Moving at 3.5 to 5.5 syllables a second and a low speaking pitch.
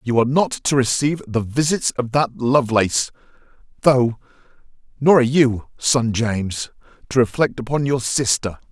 Yes: 5.1 syllables/s; low, 125 Hz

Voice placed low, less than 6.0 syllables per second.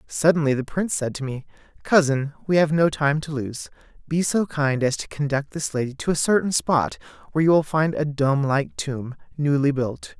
No: medium, 145 Hz; 5.1 syllables/s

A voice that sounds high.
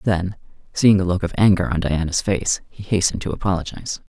No: very low, 90 Hz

